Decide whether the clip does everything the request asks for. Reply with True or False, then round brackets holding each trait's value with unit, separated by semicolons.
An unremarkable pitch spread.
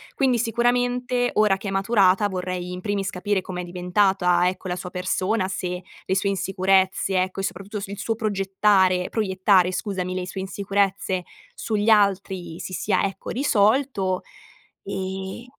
False (2.1 semitones)